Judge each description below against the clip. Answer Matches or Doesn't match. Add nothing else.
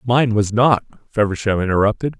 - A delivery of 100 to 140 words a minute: Matches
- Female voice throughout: Doesn't match